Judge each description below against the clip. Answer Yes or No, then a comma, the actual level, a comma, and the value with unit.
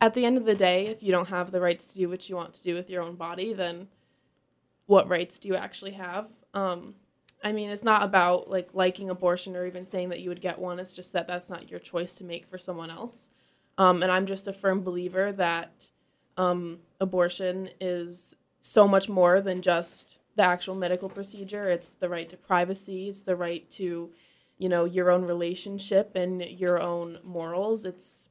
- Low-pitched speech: No, medium, 180 Hz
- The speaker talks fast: Yes, fast, 210 wpm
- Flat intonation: Yes, narrow, 1.6 semitones